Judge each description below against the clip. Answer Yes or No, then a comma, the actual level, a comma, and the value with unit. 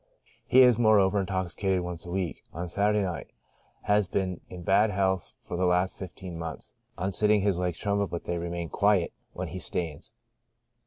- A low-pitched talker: Yes, very low, 95 Hz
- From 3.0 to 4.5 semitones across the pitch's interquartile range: No, narrow, 2.5 semitones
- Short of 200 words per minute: Yes, average, 180 wpm